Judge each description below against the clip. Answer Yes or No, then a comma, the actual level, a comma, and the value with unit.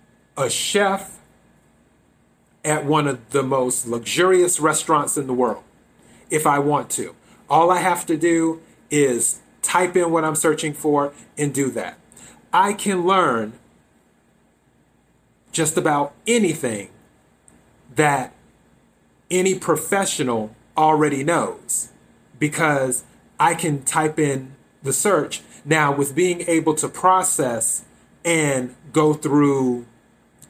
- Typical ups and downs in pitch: Yes, average, 3.5 semitones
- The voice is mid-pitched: Yes, medium, 155 Hz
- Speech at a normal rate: No, slow, 115 wpm